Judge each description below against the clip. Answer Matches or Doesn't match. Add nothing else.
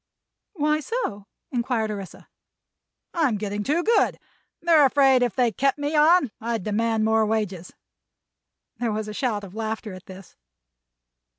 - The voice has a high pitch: Matches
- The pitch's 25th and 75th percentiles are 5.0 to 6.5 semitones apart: Matches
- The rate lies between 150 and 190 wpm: Doesn't match